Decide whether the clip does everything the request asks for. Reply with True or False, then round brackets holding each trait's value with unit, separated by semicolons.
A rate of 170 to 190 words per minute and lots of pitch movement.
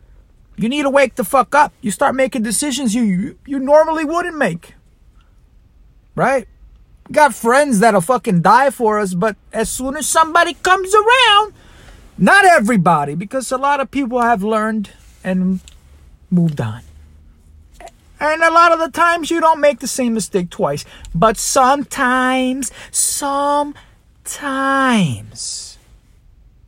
False (135 wpm; 6.7 semitones)